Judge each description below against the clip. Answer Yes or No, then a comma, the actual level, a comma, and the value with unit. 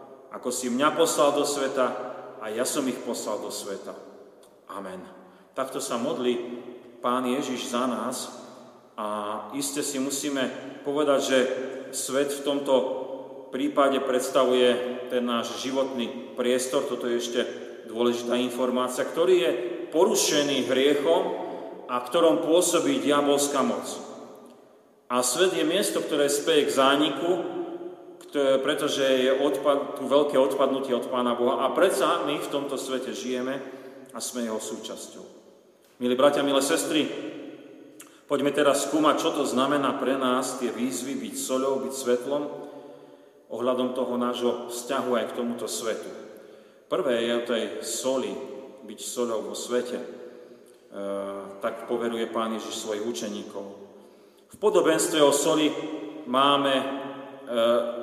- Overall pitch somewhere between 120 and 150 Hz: Yes, low, 130 Hz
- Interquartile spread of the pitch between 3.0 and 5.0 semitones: No, narrow, 2.5 semitones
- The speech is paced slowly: No, average, 130 wpm